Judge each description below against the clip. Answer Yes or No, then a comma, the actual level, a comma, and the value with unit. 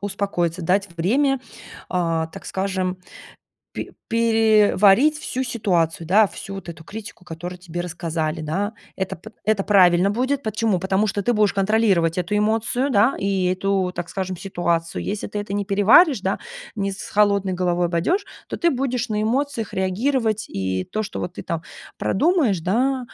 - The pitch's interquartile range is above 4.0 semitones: No, average, 3.7 semitones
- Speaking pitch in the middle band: No, high, 195 Hz